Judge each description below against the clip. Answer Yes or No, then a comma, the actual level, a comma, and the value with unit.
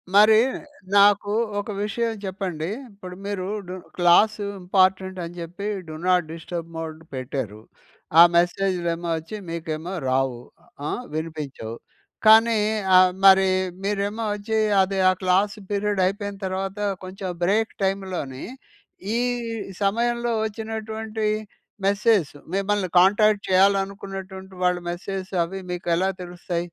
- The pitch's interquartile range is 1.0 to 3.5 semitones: Yes, average, 2.8 semitones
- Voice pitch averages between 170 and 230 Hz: Yes, high, 190 Hz